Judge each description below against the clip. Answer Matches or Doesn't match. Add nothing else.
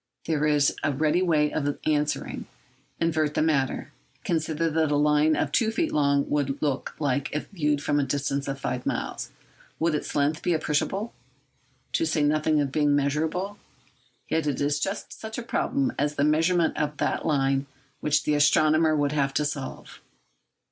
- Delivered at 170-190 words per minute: Matches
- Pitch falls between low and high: Matches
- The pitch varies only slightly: Matches